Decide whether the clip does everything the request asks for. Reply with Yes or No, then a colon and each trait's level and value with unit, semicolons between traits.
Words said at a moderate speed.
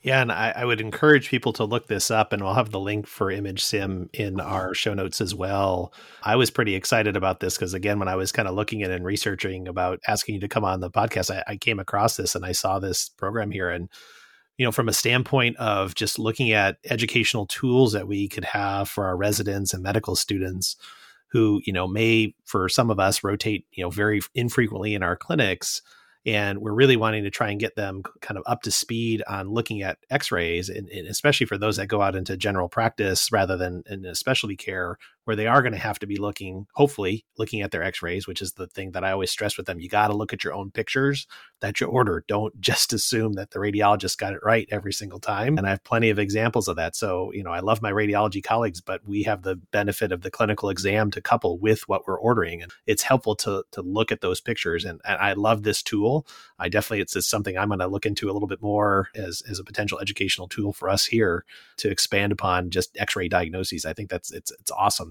No: fast, 240 wpm